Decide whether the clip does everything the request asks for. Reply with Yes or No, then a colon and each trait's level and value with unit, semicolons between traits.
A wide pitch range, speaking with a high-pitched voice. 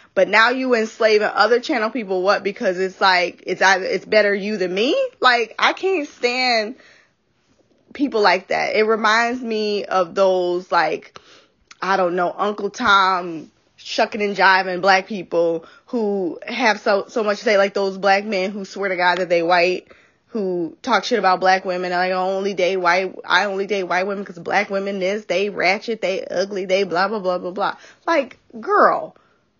No: average, 2.7 semitones; high, 195 Hz